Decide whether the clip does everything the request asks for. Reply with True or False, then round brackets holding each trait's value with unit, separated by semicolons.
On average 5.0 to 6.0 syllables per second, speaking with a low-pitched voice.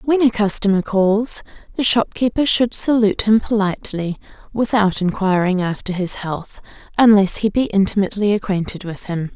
False (5.1 syllables/s; 205 Hz)